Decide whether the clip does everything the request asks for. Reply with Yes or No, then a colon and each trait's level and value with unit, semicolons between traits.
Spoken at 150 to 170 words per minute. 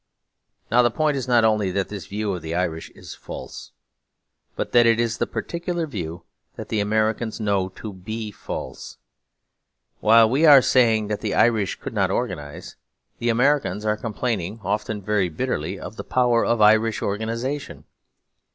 Yes: average, 165 wpm